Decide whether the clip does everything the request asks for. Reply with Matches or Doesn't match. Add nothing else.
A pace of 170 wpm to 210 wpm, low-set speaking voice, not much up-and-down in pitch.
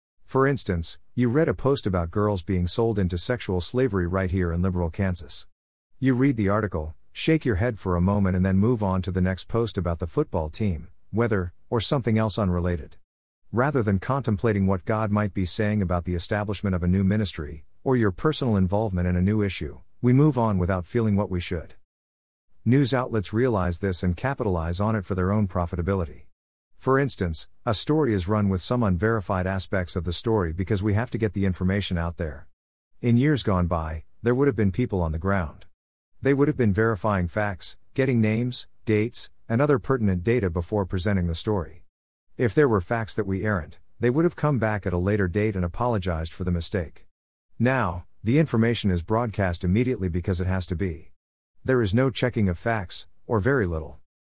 Doesn't match